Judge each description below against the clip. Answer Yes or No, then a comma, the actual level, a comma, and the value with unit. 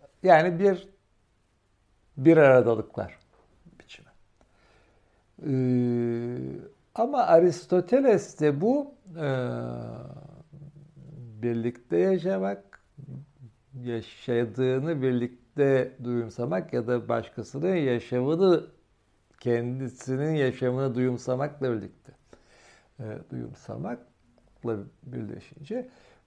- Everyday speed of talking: No, slow, 60 wpm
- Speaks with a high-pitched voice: No, low, 125 Hz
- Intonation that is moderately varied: Yes, average, 4.5 semitones